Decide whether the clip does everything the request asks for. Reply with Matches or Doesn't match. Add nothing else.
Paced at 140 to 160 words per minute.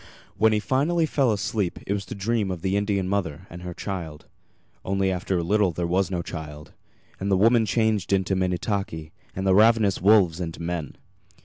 Doesn't match